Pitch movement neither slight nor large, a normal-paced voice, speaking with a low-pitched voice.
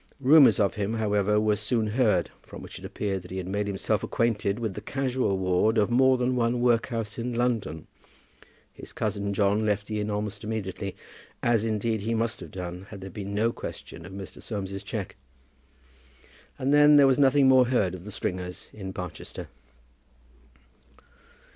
Yes: average, 3.3 semitones; average, 175 wpm; low, 105 Hz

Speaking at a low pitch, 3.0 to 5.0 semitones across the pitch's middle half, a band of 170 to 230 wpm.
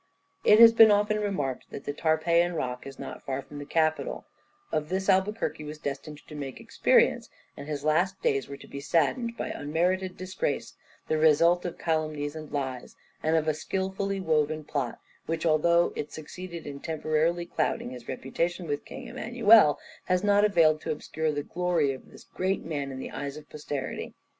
No: medium, 155 Hz; average, 4.0 semitones; average, 180 wpm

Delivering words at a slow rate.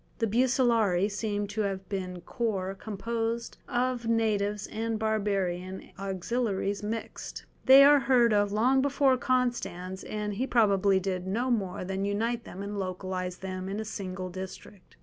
No: average, 150 wpm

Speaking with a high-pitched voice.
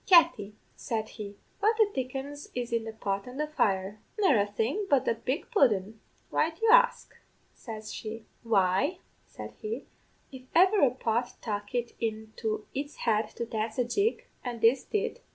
Yes: high, 235 Hz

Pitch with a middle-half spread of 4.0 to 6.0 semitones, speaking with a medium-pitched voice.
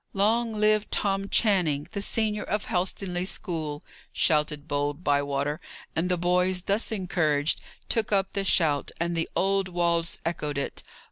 Yes: average, 4.6 semitones; medium, 180 Hz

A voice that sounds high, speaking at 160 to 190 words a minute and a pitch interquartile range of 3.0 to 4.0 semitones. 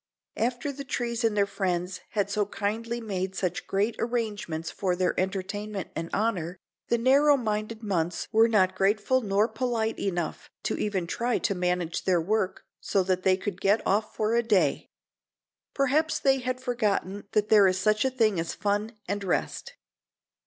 Yes: high, 210 Hz; average, 170 wpm; average, 3.7 semitones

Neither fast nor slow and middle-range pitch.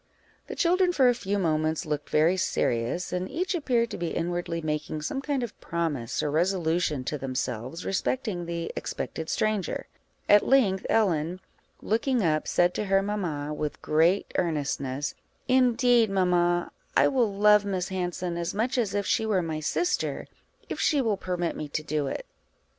Yes: average, 165 wpm; medium, 180 Hz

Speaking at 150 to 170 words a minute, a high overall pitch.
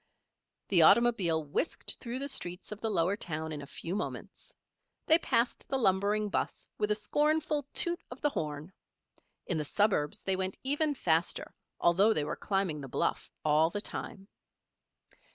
Yes: average, 165 wpm; high, 195 Hz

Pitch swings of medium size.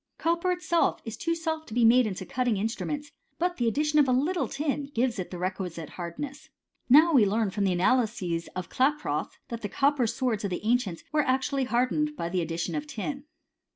No: wide, 7.2 semitones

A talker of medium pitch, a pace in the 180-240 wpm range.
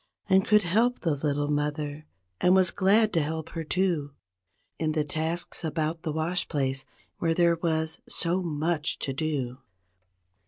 No: medium, 160 Hz; average, 155 wpm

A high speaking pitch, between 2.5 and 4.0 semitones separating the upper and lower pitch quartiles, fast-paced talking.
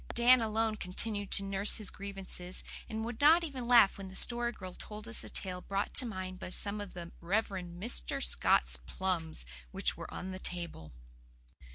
No: high, 195 Hz; average, 3.6 semitones; average, 185 wpm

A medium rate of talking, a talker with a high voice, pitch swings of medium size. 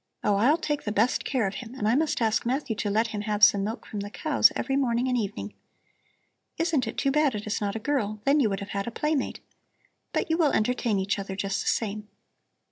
No: fast, 235 wpm; high, 225 Hz; average, 4.7 semitones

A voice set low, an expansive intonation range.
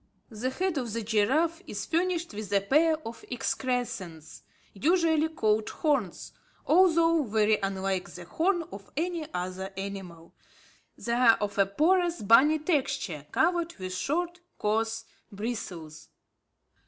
No: high, 230 Hz; wide, 8.4 semitones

